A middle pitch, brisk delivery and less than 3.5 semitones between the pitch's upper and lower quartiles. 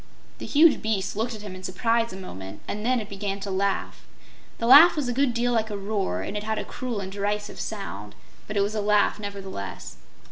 No: high, 210 Hz; fast, 225 wpm; average, 2.8 semitones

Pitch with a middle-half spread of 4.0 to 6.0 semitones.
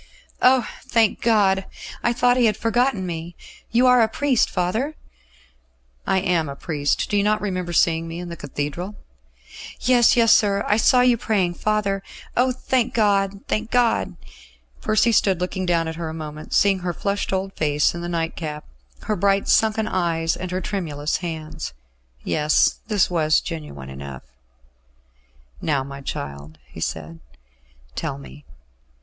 Yes: average, 5.3 semitones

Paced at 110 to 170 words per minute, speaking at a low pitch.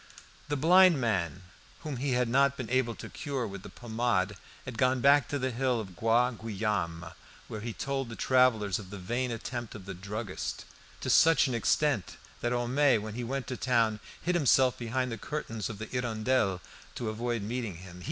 No: average, 190 wpm; low, 120 Hz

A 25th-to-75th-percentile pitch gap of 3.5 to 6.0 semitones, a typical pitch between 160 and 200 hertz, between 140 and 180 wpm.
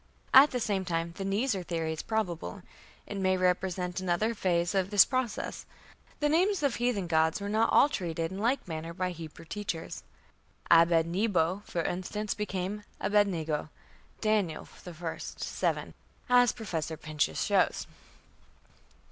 Yes: average, 4.2 semitones; medium, 185 Hz; average, 150 wpm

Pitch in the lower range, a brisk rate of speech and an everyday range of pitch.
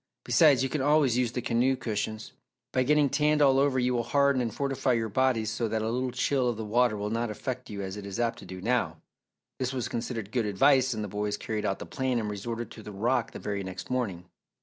Yes: low, 120 Hz; fast, 245 wpm; average, 3.5 semitones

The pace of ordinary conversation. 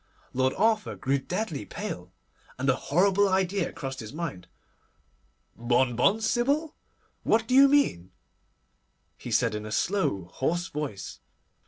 No: slow, 130 wpm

